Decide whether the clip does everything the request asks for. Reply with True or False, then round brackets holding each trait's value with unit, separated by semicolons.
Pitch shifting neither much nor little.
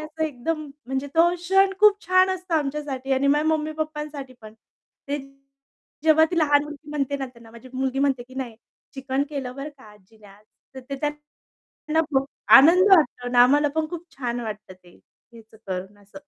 True (3.9 semitones)